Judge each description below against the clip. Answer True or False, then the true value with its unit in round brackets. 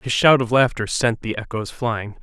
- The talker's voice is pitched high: False (115 Hz)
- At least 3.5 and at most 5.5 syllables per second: True (4.6 syllables/s)